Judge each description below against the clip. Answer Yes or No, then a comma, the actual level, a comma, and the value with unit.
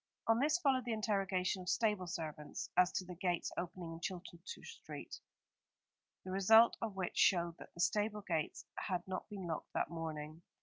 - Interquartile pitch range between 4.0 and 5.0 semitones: No, average, 3.5 semitones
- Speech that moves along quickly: No, average, 175 wpm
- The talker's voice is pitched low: No, medium, 185 Hz